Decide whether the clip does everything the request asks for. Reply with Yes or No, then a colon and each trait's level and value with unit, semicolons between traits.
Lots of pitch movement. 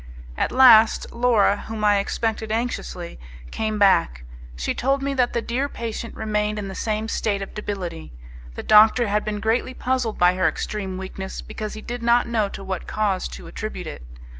No: average, 3.0 semitones